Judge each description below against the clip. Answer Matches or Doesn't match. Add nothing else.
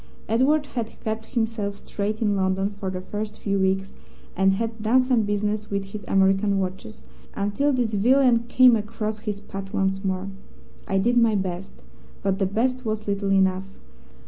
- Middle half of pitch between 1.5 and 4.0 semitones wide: Matches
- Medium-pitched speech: Doesn't match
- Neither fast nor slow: Matches